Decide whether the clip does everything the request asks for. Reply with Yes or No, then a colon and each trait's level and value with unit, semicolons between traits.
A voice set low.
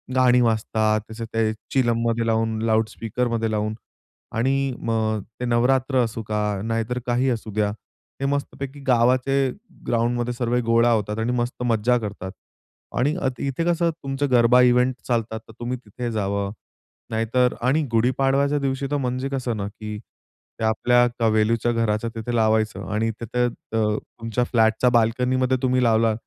Yes: low, 120 Hz